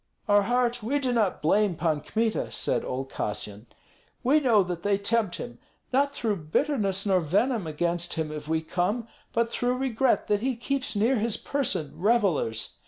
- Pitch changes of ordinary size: No, wide, 6.6 semitones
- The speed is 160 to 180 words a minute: Yes, average, 170 wpm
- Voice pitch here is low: No, high, 205 Hz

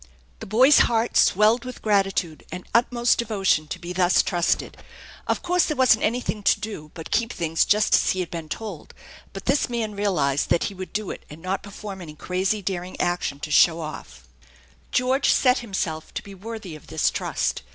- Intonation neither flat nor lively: Yes, average, 4.7 semitones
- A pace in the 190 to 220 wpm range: Yes, average, 195 wpm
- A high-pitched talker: Yes, high, 195 Hz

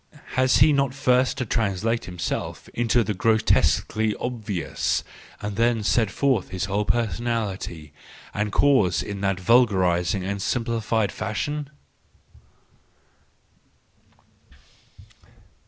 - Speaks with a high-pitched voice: No, low, 110 Hz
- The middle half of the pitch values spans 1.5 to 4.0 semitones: Yes, average, 3.7 semitones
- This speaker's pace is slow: Yes, slow, 100 wpm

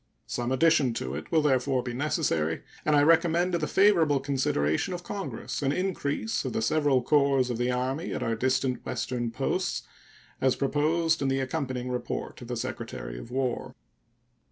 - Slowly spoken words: No, average, 175 wpm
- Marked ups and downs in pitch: No, average, 4.0 semitones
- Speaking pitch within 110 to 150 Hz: Yes, low, 135 Hz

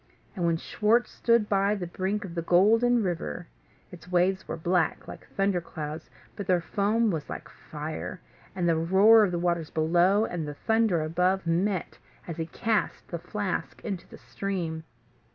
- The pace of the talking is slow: No, average, 170 wpm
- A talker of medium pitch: Yes, medium, 180 Hz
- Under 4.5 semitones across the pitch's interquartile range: Yes, average, 3.4 semitones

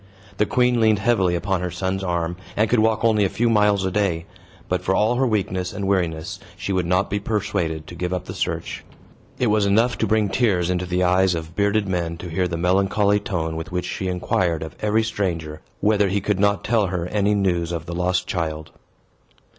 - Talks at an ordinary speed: No, fast, 215 wpm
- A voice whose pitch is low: Yes, very low, 95 Hz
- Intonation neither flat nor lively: Yes, average, 3.0 semitones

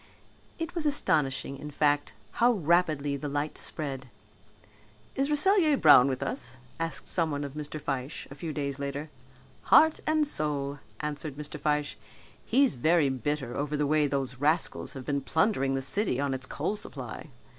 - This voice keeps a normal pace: Yes, average, 160 wpm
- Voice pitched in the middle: Yes, medium, 150 Hz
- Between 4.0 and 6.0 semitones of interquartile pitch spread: No, average, 3.1 semitones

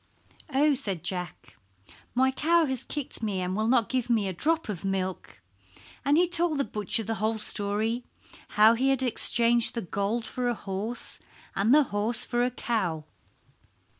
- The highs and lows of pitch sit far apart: No, average, 4.5 semitones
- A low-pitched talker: No, high, 230 Hz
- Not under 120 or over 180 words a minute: Yes, average, 170 wpm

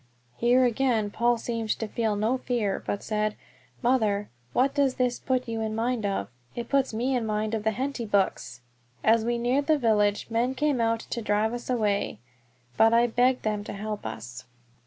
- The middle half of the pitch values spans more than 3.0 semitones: No, average, 2.7 semitones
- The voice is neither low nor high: No, high, 225 Hz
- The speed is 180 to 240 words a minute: Yes, average, 190 wpm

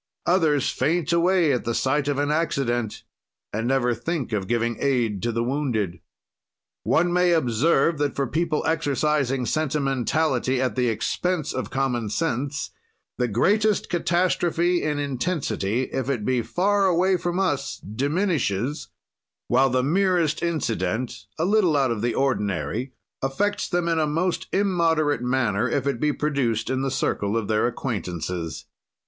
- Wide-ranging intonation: Yes, wide, 5.7 semitones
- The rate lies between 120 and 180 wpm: Yes, average, 145 wpm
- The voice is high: No, low, 135 Hz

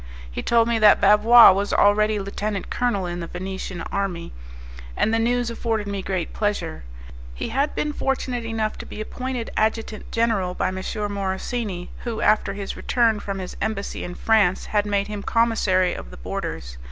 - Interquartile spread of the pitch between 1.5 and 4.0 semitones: Yes, average, 3.0 semitones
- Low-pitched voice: No, high, 210 Hz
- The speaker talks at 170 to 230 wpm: Yes, average, 175 wpm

